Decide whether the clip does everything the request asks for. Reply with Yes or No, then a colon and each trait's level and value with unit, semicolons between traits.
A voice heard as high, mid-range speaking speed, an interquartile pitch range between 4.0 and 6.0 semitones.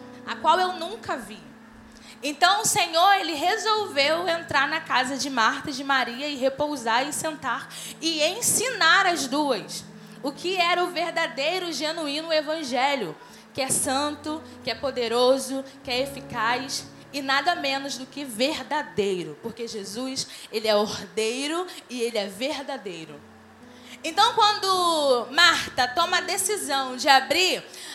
Yes: very high, 280 Hz; average, 140 wpm; average, 5.2 semitones